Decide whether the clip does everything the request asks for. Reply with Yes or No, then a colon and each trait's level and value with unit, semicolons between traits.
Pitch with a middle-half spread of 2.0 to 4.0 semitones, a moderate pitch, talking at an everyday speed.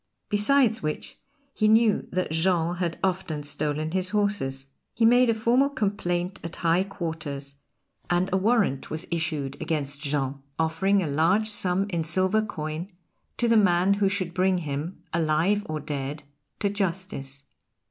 No: average, 4.7 semitones; medium, 175 Hz; average, 150 wpm